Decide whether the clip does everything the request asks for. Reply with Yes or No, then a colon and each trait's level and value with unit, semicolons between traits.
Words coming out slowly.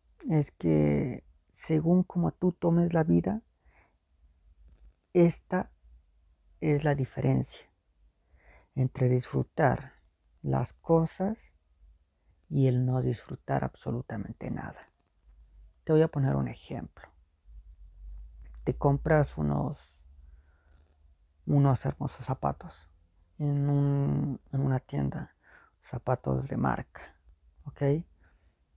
Yes: slow, 90 wpm